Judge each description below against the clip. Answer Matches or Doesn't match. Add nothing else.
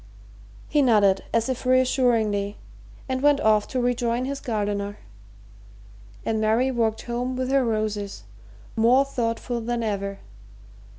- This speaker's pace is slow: Matches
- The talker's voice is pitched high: Matches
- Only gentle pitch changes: Doesn't match